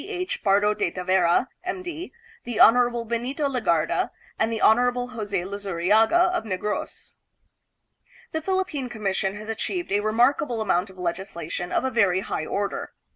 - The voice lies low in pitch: No, high, 220 Hz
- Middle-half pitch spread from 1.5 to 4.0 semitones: No, average, 4.7 semitones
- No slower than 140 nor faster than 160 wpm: Yes, average, 150 wpm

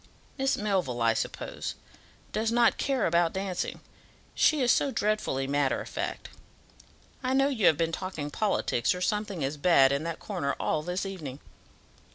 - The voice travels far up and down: Yes, wide, 6.7 semitones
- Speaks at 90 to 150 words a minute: No, average, 165 wpm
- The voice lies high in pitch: No, medium, 180 Hz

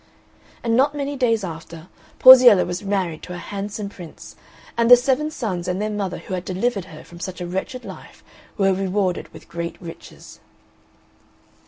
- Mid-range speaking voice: No, high, 195 Hz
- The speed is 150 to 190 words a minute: Yes, average, 170 wpm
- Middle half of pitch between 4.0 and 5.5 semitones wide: Yes, average, 4.8 semitones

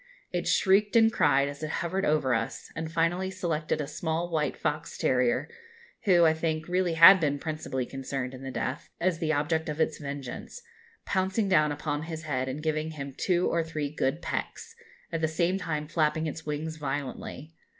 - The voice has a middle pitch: Yes, medium, 155 Hz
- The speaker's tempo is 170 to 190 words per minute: Yes, average, 185 wpm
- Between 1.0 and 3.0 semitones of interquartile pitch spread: Yes, average, 2.7 semitones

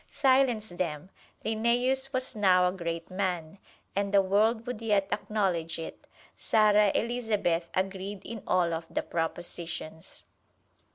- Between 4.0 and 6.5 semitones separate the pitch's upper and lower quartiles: Yes, average, 4.3 semitones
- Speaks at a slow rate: Yes, slow, 125 wpm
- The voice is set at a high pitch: Yes, high, 200 Hz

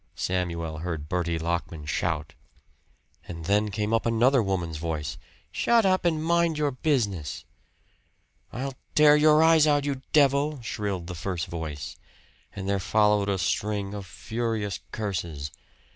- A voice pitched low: Yes, low, 100 Hz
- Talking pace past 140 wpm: No, slow, 135 wpm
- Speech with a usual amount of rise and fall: No, wide, 8.4 semitones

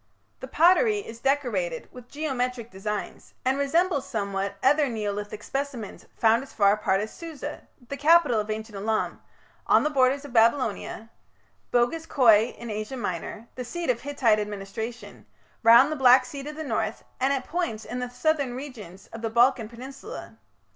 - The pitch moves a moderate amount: Yes, average, 4.4 semitones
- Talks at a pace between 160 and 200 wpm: Yes, average, 165 wpm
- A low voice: No, high, 245 Hz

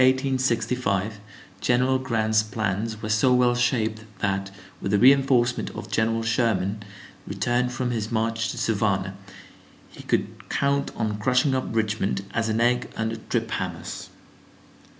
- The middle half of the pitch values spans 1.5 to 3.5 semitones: Yes, narrow, 2.6 semitones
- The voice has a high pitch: No, low, 115 Hz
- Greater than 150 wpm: No, average, 145 wpm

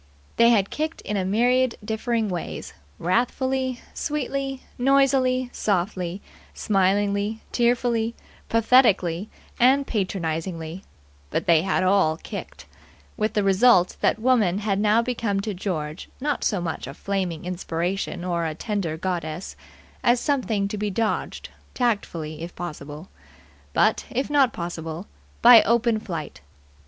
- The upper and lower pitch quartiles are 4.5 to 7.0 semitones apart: Yes, wide, 5.4 semitones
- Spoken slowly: Yes, slow, 125 wpm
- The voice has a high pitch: Yes, high, 205 Hz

